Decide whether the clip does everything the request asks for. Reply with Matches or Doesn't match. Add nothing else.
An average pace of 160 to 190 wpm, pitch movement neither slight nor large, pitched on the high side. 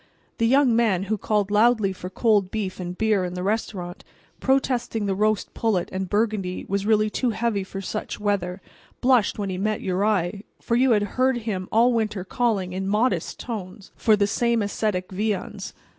Matches